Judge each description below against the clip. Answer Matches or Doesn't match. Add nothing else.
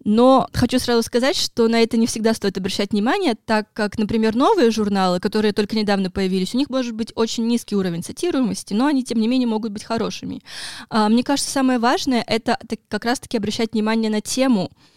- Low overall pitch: Doesn't match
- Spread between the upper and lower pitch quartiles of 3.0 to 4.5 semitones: Doesn't match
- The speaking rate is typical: Doesn't match